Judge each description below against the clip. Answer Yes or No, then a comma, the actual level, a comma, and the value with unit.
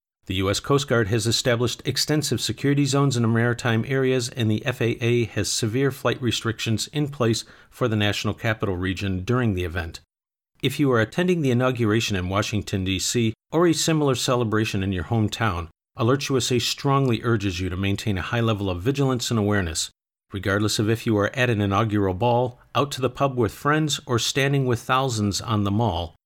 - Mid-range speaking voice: No, low, 115 Hz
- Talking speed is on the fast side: No, average, 185 wpm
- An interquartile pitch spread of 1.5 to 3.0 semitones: No, average, 3.8 semitones